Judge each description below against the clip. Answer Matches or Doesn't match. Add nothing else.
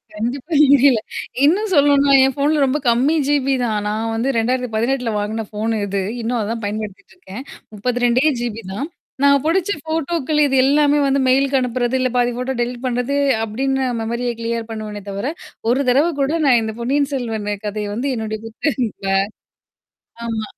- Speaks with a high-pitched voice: Matches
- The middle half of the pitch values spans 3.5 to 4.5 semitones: Matches